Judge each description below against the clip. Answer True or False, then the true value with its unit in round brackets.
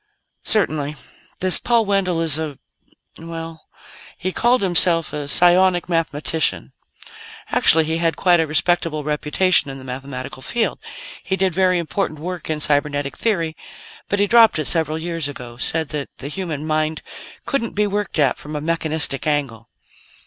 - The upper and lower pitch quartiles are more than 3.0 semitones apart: True (3.6 semitones)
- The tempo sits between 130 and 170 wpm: True (155 wpm)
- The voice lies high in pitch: False (160 Hz)